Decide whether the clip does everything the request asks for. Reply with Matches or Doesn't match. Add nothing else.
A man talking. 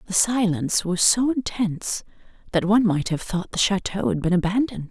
Doesn't match